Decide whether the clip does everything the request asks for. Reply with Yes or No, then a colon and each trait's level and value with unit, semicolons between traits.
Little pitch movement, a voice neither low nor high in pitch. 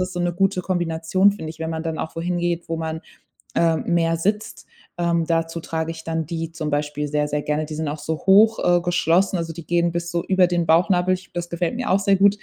Yes: narrow, 1.9 semitones; medium, 170 Hz